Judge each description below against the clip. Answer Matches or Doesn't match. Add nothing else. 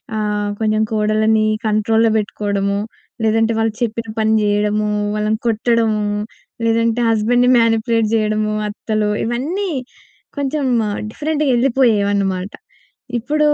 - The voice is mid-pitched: Doesn't match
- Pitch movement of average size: Doesn't match